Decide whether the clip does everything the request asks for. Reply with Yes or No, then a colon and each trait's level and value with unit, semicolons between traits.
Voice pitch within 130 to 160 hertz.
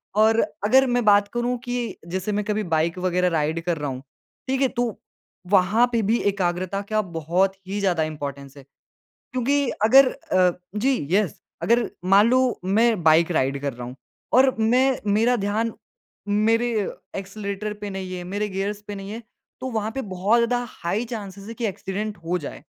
No: high, 205 Hz